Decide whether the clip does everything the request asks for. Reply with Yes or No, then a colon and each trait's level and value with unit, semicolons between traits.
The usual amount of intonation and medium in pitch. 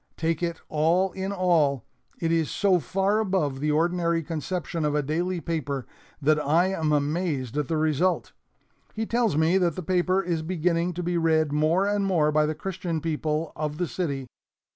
Yes: average, 3.0 semitones; medium, 165 Hz